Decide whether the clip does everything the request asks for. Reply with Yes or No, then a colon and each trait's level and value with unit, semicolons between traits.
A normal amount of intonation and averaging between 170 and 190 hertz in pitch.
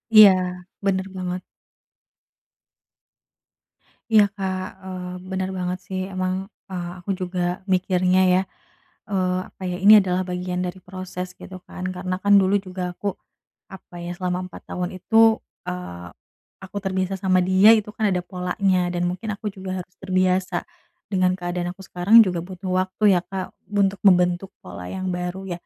No: narrow, 1.1 semitones; medium, 185 Hz